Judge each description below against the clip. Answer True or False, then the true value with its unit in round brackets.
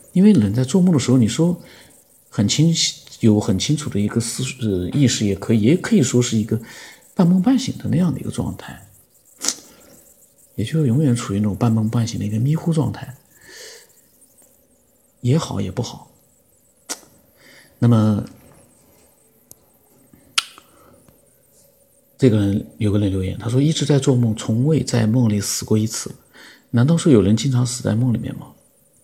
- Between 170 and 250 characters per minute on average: True (225 characters per minute)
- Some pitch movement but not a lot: True (4.9 semitones)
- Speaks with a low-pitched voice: True (120 Hz)